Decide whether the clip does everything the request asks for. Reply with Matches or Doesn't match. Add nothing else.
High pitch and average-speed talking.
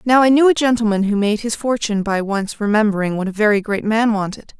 Doesn't match